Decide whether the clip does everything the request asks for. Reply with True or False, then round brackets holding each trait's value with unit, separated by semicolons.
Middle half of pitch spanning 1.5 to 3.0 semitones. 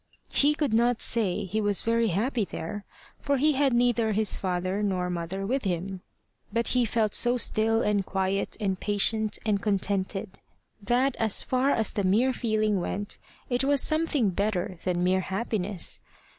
False (3.9 semitones)